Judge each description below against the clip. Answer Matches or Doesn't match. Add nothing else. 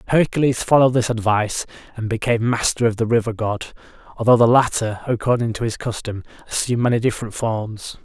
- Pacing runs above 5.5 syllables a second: Matches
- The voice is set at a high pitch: Doesn't match